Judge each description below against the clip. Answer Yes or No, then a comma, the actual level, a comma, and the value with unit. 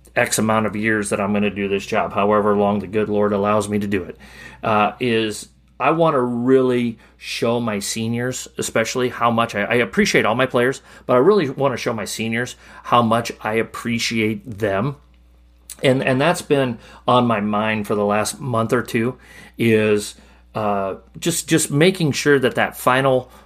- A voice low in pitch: Yes, low, 115 Hz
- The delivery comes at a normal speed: Yes, average, 190 wpm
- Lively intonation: No, average, 3.3 semitones